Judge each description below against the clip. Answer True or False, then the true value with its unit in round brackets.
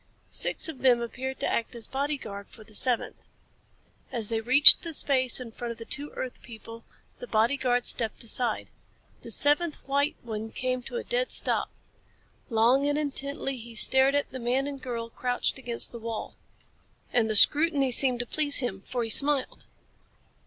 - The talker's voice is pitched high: True (255 Hz)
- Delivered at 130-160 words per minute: False (175 wpm)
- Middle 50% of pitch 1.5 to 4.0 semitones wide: True (3.4 semitones)